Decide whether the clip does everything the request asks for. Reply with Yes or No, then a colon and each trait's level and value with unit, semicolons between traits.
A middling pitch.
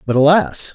Yes: medium, 155 Hz